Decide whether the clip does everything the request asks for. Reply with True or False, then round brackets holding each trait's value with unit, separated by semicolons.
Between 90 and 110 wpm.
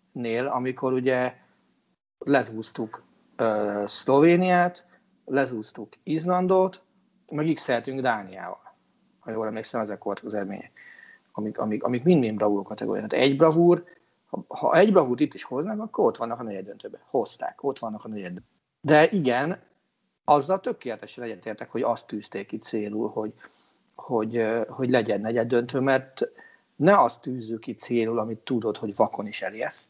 False (145 wpm)